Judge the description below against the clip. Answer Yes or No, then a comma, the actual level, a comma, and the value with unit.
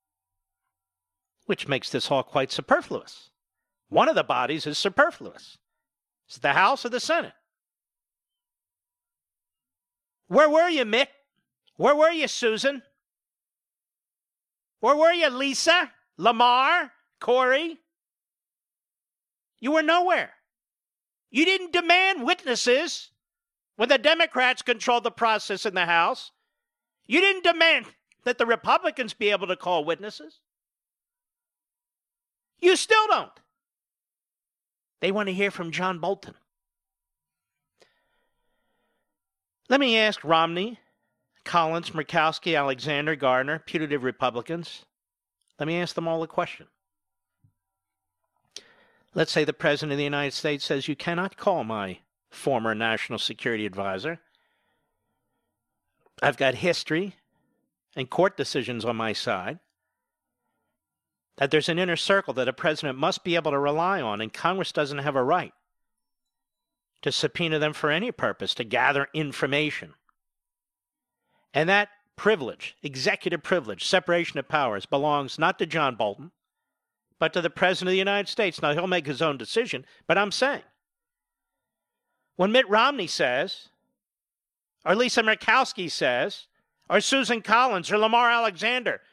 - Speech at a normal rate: No, slow, 125 wpm